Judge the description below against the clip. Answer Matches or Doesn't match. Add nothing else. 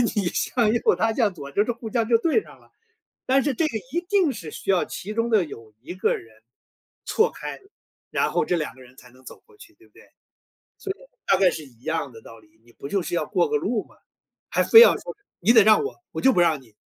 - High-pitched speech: Matches